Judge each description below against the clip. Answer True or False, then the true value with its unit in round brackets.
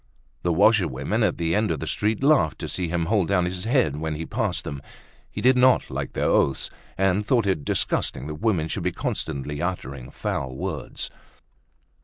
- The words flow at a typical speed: True (190 wpm)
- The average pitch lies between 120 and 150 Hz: False (90 Hz)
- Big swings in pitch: True (5.8 semitones)